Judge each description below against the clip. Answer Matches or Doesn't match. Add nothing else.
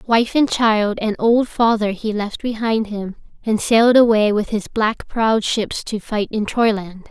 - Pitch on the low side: Doesn't match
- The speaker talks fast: Doesn't match